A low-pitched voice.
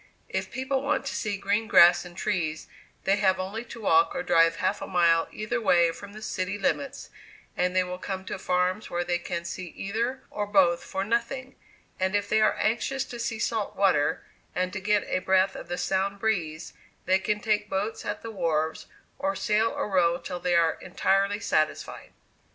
No: high, 195 Hz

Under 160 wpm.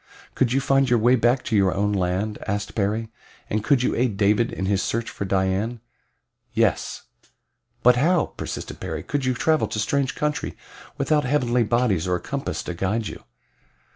No: average, 180 wpm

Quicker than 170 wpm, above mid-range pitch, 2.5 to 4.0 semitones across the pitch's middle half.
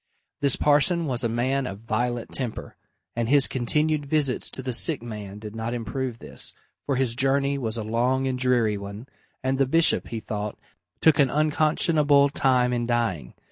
No: average, 180 wpm; low, 125 Hz; average, 3.4 semitones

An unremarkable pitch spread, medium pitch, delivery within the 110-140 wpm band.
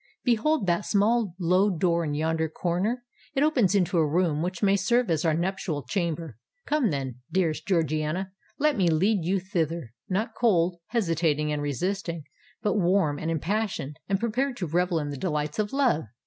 No: average, 4.3 semitones; medium, 180 Hz; average, 160 wpm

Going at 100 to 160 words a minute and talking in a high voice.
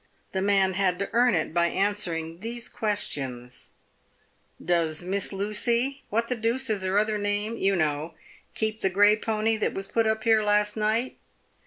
No: average, 190 wpm; high, 205 Hz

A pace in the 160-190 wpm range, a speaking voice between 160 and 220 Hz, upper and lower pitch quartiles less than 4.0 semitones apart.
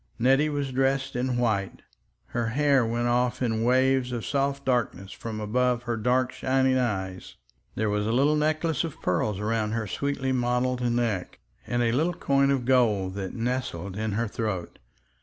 No: average, 170 wpm; low, 125 Hz; average, 3.3 semitones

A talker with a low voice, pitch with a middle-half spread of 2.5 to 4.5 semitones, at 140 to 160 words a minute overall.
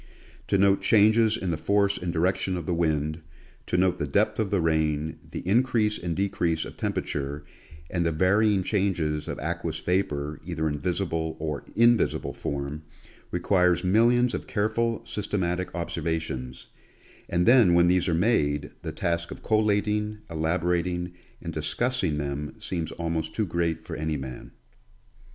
Yes: very low, 85 Hz; average, 4.2 semitones; average, 155 wpm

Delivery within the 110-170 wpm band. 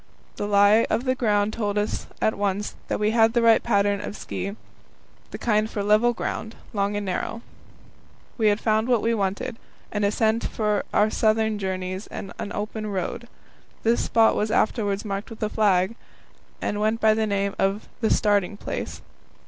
No: average, 180 wpm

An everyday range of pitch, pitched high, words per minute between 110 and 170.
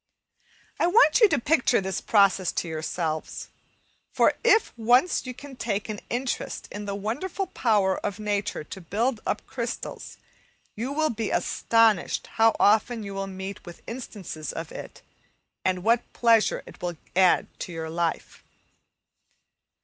Yes: average, 4.2 semitones; high, 210 Hz; average, 150 wpm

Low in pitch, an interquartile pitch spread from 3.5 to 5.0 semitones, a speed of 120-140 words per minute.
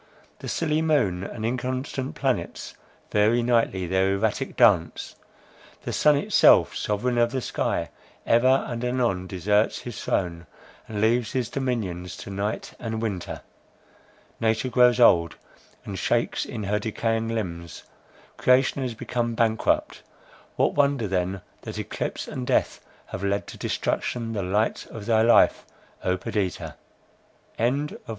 Yes: low, 115 Hz; average, 4.0 semitones; slow, 135 wpm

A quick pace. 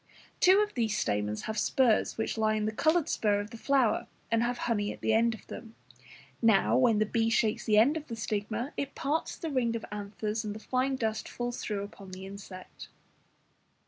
Yes: fast, 210 wpm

